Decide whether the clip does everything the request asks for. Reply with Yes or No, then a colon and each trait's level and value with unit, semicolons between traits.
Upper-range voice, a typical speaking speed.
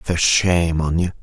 No: very low, 85 Hz; average, 195 wpm